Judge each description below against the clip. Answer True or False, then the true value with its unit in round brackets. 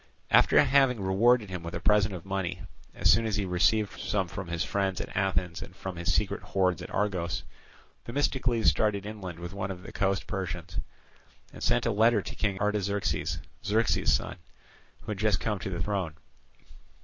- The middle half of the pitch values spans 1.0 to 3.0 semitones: True (2.6 semitones)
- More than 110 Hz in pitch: False (95 Hz)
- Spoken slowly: False (185 wpm)